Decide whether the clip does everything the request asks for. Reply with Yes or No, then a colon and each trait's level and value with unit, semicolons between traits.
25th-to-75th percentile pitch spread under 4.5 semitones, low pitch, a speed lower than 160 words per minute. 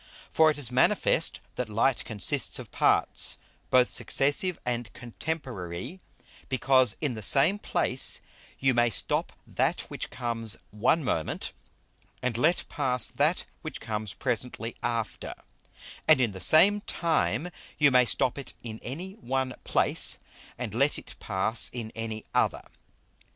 Yes: average, 4.0 semitones; low, 125 Hz; average, 140 wpm